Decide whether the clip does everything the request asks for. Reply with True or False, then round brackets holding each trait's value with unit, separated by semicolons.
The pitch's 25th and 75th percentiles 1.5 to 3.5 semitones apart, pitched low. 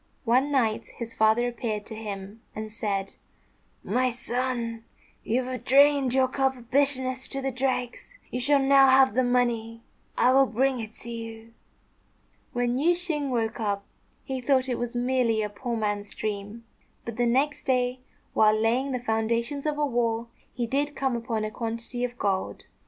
False (2.8 semitones; 245 Hz)